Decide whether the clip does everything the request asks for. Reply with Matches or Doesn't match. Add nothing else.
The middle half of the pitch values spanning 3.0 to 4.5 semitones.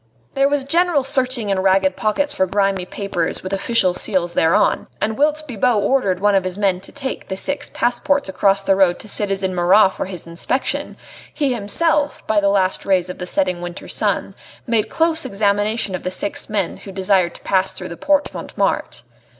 Doesn't match